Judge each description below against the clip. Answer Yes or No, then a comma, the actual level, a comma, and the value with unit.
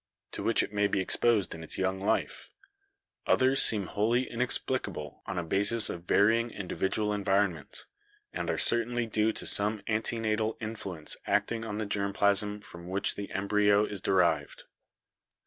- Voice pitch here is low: Yes, low, 105 Hz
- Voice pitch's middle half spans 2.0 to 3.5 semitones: Yes, narrow, 2.4 semitones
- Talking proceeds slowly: No, average, 160 wpm